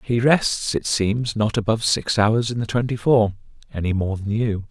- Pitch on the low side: Yes, low, 110 Hz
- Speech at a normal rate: Yes, average, 190 wpm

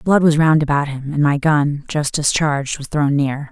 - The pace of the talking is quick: Yes, fast, 220 wpm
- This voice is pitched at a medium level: Yes, medium, 145 Hz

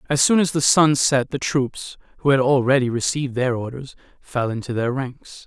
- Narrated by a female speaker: No, male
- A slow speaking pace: No, average, 200 wpm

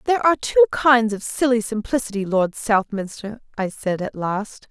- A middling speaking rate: Yes, average, 165 wpm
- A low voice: No, high, 225 Hz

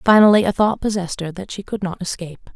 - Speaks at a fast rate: Yes, fast, 235 wpm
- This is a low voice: No, high, 190 Hz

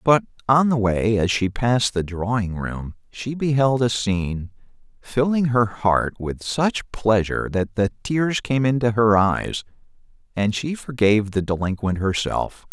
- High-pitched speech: No, low, 110 Hz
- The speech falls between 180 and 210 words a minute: No, average, 155 wpm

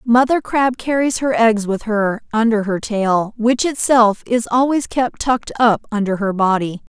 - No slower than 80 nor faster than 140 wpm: No, average, 170 wpm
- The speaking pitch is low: No, high, 225 Hz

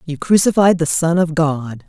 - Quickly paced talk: No, average, 190 wpm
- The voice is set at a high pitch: No, medium, 165 Hz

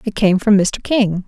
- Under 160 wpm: No, fast, 235 wpm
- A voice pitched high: Yes, high, 205 Hz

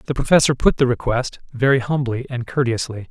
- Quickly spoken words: No, average, 175 wpm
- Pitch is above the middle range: No, low, 125 Hz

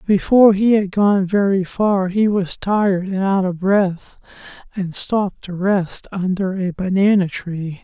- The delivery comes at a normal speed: Yes, average, 160 wpm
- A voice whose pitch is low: No, high, 190 Hz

